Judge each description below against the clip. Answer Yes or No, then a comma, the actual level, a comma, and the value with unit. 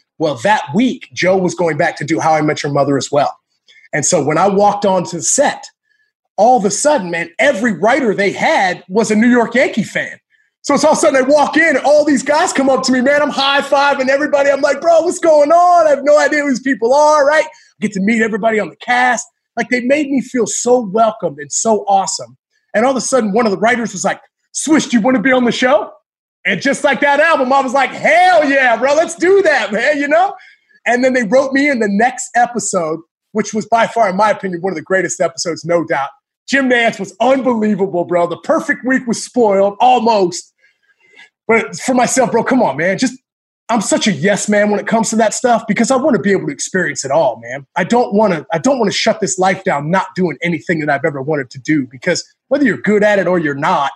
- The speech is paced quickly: Yes, fast, 250 wpm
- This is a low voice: No, high, 240 Hz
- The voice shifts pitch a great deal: Yes, wide, 6.7 semitones